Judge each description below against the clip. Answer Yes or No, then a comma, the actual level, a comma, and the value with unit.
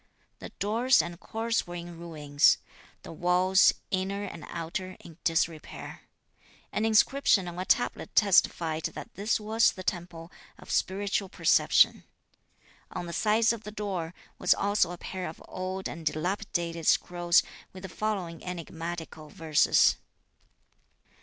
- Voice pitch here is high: No, medium, 180 Hz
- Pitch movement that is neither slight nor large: Yes, average, 3.3 semitones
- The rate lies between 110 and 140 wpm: Yes, slow, 135 wpm